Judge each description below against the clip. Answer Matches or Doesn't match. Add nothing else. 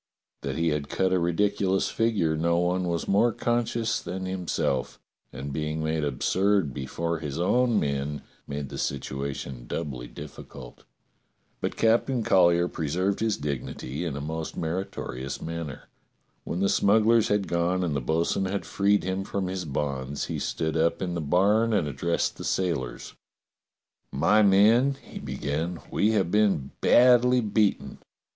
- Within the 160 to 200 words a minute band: Doesn't match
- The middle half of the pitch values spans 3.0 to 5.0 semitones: Doesn't match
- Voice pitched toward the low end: Matches